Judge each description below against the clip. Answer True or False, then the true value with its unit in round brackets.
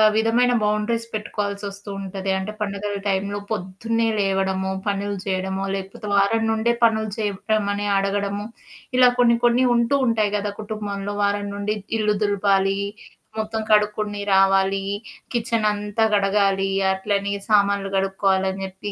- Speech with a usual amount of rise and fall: False (1.6 semitones)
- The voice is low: False (205 Hz)